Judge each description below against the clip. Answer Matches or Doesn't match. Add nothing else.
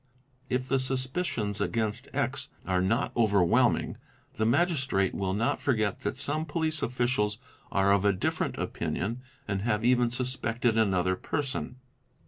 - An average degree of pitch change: Matches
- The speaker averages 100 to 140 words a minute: Matches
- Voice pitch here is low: Matches